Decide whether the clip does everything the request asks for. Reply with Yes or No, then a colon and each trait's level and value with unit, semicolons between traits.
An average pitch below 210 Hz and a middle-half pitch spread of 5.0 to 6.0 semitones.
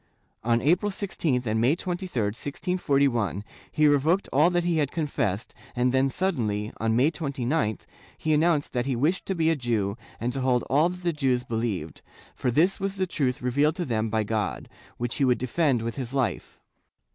Yes: low, 135 Hz; wide, 5.6 semitones